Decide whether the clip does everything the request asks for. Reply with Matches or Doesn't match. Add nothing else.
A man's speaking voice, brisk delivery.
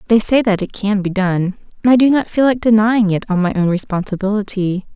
Doesn't match